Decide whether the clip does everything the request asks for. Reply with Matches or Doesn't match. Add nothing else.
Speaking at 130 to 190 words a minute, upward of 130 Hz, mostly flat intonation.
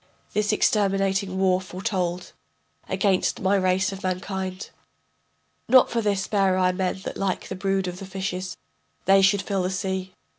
Matches